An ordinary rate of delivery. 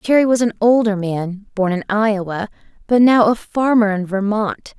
Yes: average, 175 wpm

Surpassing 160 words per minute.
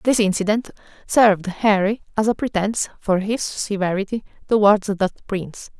No: slow, 135 wpm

